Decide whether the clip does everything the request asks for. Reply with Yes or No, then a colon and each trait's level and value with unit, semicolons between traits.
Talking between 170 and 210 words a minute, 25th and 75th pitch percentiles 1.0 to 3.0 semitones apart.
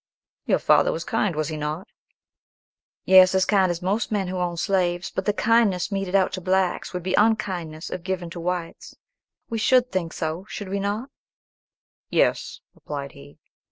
Yes: average, 175 wpm; narrow, 2.6 semitones